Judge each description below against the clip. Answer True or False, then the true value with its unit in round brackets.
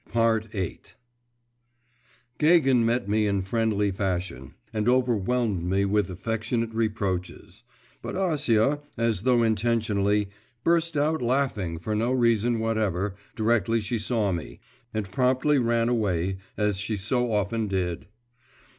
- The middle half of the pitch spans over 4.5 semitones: False (3.3 semitones)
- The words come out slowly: True (120 wpm)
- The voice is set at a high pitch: False (110 Hz)